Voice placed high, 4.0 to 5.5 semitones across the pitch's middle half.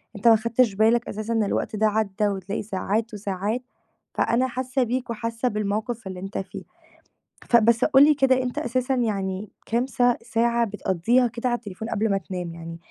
No: high, 225 Hz; average, 3.2 semitones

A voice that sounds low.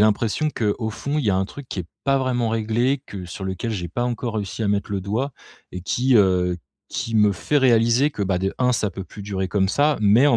Yes: low, 110 Hz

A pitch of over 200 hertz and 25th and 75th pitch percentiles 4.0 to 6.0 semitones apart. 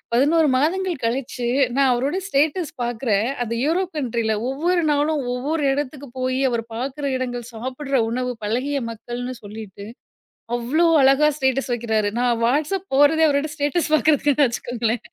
No: very high, 265 Hz; average, 3.5 semitones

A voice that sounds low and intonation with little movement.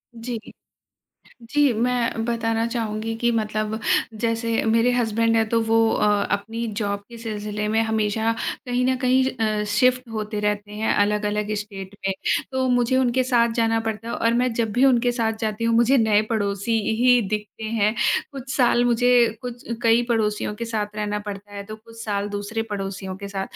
No: high, 225 Hz; narrow, 2.1 semitones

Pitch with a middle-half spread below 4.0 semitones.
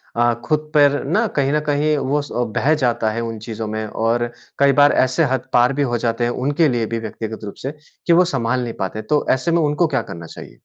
No: average, 4.4 semitones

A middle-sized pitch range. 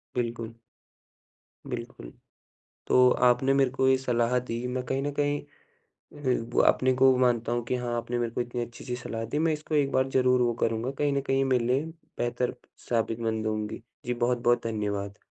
No: narrow, 2.0 semitones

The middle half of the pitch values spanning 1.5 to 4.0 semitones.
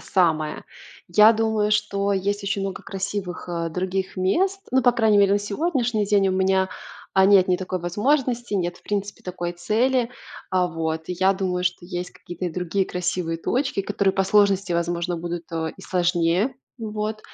Yes: average, 2.9 semitones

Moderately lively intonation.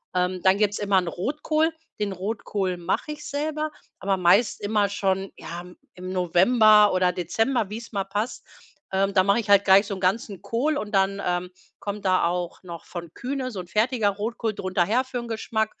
Yes: average, 3.4 semitones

